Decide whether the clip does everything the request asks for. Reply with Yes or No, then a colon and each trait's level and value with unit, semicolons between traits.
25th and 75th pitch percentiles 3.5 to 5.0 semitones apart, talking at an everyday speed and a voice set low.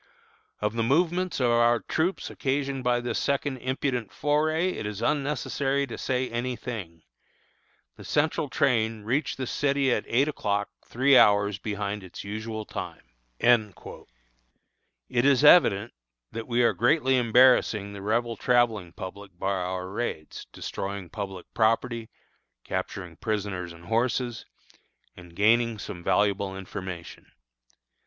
No: average, 4.5 semitones; slow, 130 wpm; low, 115 Hz